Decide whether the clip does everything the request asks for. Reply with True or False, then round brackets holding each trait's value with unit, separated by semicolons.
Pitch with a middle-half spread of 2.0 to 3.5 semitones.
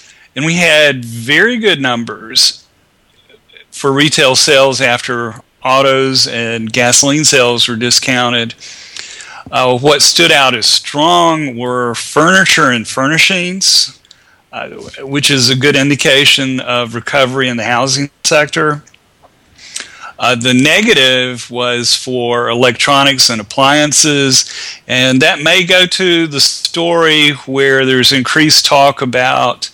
True (3.2 semitones)